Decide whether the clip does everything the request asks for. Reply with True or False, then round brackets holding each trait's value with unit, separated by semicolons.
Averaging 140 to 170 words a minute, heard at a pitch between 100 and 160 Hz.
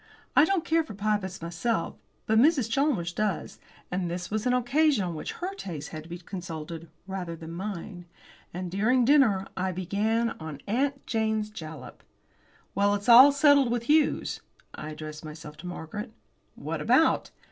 False (165 wpm; 200 Hz)